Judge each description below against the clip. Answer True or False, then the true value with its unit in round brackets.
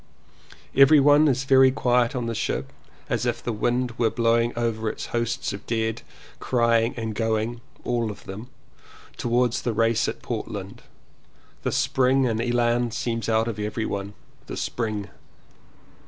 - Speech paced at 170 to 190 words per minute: False (150 wpm)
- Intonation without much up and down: True (1.6 semitones)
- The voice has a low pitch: True (115 Hz)